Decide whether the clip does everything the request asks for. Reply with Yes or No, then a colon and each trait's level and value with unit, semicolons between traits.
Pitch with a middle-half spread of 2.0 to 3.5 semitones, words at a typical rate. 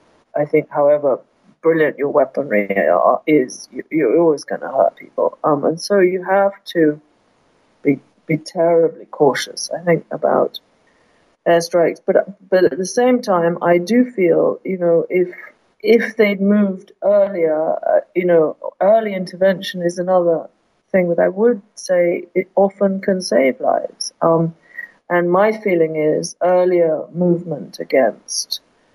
Yes: average, 3.1 semitones; average, 145 wpm